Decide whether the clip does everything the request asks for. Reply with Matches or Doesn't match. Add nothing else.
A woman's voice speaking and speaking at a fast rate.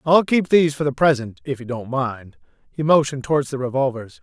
Doesn't match